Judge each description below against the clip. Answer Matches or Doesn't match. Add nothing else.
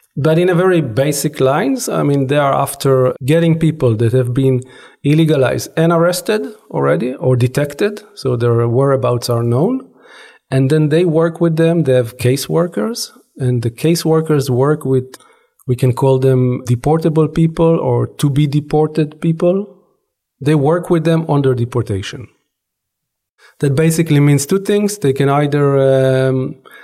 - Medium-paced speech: Matches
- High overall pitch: Doesn't match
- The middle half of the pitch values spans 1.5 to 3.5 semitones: Doesn't match